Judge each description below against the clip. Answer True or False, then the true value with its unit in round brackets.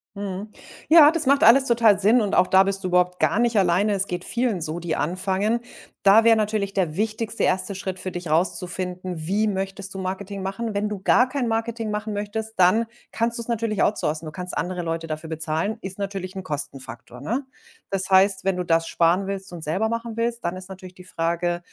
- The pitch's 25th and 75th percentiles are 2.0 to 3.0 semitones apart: False (3.5 semitones)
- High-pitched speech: True (195 Hz)